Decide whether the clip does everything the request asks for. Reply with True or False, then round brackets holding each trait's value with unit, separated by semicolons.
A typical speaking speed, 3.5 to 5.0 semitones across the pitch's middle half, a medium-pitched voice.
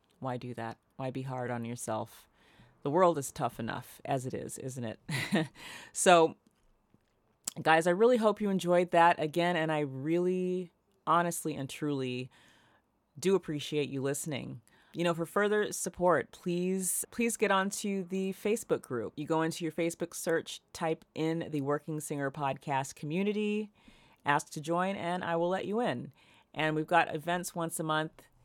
True (165 wpm; 4.1 semitones; 165 Hz)